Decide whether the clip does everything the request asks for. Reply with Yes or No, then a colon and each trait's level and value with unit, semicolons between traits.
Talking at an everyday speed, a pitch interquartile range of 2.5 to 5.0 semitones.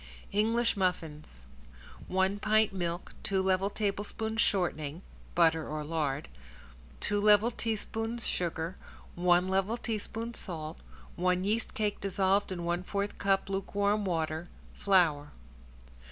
No: slow, 115 wpm; average, 3.4 semitones